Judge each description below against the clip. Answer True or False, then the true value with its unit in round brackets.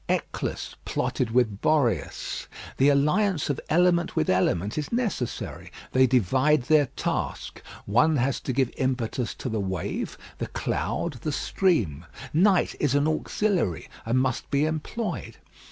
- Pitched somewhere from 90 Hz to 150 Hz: True (135 Hz)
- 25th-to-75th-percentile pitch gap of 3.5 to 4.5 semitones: False (5.1 semitones)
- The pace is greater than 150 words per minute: False (135 wpm)